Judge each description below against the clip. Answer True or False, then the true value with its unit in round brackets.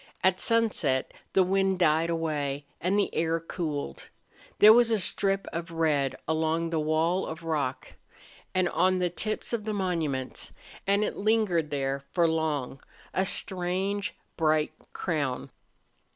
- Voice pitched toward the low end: False (165 Hz)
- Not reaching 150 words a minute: True (140 wpm)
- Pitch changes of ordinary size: True (3.8 semitones)